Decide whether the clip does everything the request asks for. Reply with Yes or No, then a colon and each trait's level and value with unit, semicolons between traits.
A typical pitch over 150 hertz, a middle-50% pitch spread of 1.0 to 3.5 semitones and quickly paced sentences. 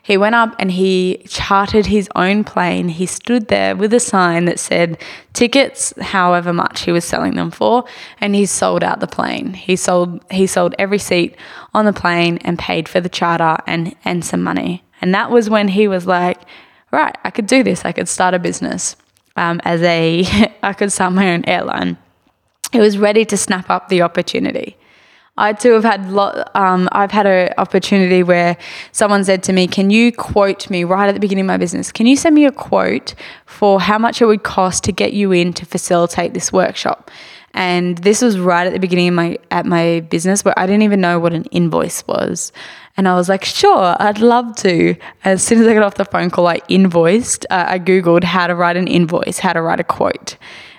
Yes: medium, 185 Hz; average, 3.1 semitones; fast, 215 wpm